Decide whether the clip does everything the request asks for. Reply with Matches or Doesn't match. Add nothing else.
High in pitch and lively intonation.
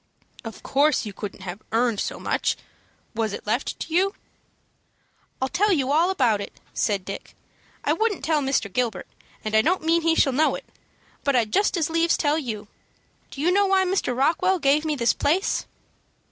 Matches